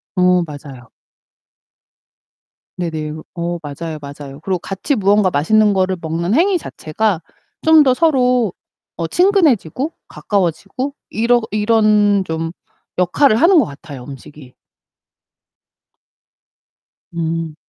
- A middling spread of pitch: No, wide, 6.5 semitones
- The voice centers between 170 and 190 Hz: Yes, medium, 185 Hz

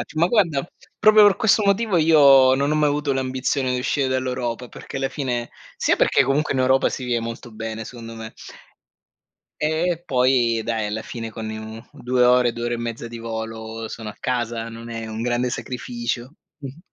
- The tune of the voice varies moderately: Yes, average, 3.2 semitones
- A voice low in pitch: Yes, low, 125 Hz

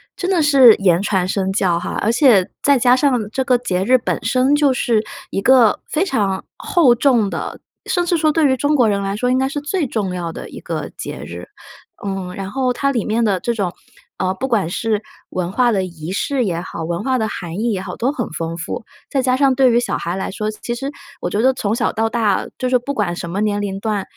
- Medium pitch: No, high, 225 Hz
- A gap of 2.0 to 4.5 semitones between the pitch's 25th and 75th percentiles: No, average, 5.2 semitones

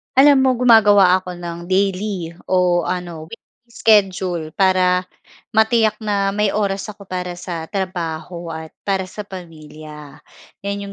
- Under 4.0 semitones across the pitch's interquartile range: Yes, average, 2.7 semitones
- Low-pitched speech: No, medium, 185 Hz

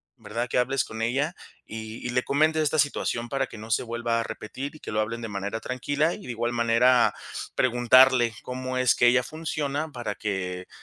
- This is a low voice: Yes, low, 120 Hz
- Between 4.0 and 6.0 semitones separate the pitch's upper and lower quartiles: No, average, 2.9 semitones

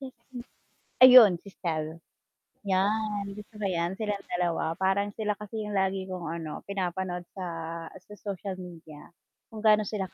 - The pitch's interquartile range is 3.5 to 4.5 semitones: No, average, 2.8 semitones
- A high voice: Yes, high, 195 Hz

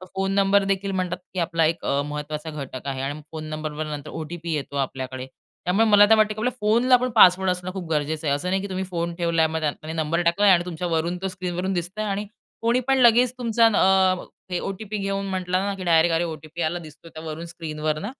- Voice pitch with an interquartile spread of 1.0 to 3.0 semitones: No, average, 3.7 semitones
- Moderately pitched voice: Yes, medium, 175 Hz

